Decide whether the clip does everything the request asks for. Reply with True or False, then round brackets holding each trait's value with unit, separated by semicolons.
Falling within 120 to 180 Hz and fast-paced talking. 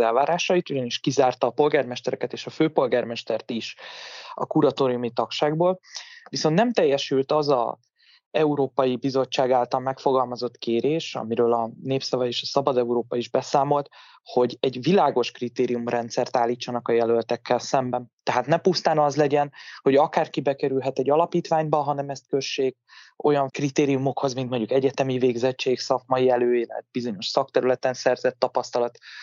False (135 Hz; 130 wpm)